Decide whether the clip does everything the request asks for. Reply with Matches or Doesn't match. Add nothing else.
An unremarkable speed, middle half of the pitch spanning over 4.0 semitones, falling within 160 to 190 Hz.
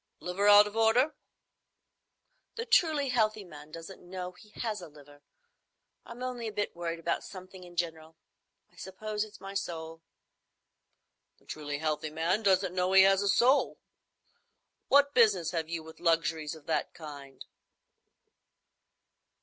Matches